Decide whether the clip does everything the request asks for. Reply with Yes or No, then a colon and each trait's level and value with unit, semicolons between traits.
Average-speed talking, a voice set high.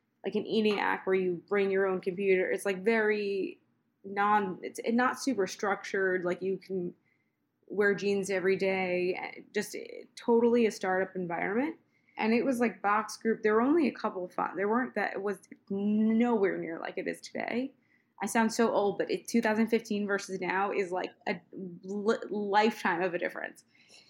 Yes: average, 180 wpm; high, 205 Hz